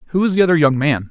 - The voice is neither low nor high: Yes, medium, 155 Hz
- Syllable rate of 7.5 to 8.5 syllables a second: Yes, 8.4 syllables/s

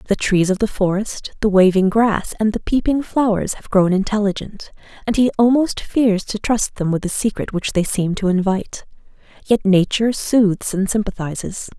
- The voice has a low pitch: No, high, 205 Hz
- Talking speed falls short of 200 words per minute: Yes, average, 180 wpm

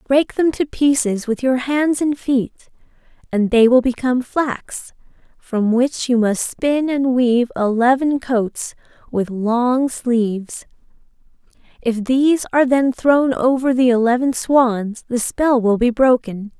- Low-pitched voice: No, very high, 250 Hz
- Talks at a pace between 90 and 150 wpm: Yes, average, 145 wpm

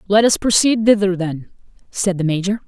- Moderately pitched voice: No, high, 195 Hz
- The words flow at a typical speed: Yes, average, 180 wpm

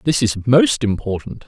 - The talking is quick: No, average, 165 wpm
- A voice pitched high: No, low, 120 Hz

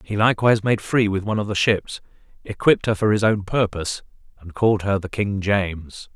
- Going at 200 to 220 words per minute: Yes, fast, 205 wpm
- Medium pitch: No, low, 100 Hz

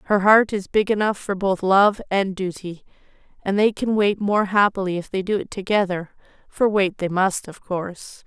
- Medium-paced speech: Yes, average, 190 wpm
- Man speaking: No, female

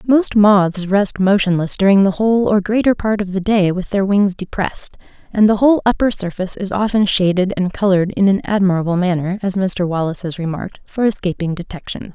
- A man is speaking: No, female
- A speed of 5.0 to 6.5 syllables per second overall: Yes, 5.7 syllables/s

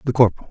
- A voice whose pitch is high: No, low, 120 Hz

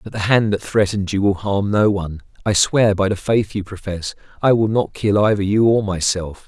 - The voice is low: Yes, low, 100 Hz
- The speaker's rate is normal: No, fast, 230 wpm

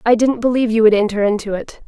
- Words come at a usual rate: No, fast, 255 wpm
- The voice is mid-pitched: No, high, 225 Hz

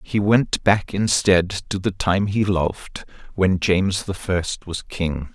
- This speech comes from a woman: No, male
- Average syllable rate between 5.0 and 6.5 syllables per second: No, 3.7 syllables/s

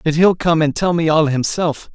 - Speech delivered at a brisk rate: Yes, fast, 245 wpm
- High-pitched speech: No, medium, 160 Hz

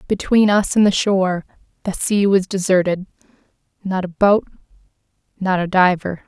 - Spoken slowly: No, average, 145 wpm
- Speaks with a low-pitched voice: No, high, 190 Hz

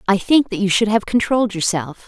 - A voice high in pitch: Yes, high, 205 Hz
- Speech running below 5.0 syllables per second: No, 5.8 syllables/s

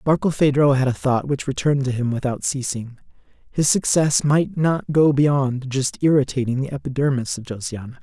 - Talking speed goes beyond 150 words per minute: Yes, average, 165 wpm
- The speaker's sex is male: Yes, male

